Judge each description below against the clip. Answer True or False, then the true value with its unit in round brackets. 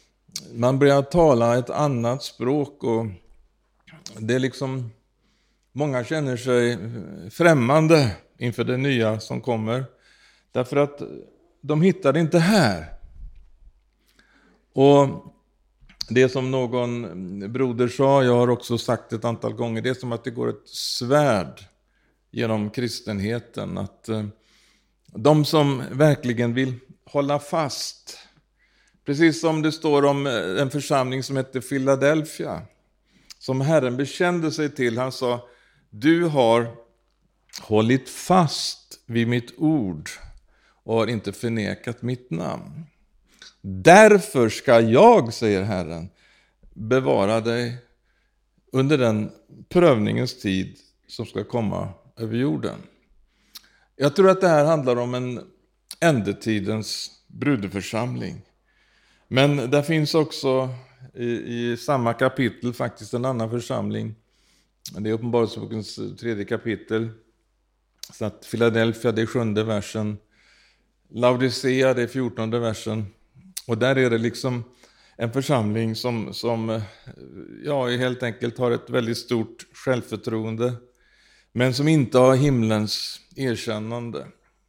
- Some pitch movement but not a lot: True (3.7 semitones)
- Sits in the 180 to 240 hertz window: False (125 Hz)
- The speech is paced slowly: True (115 wpm)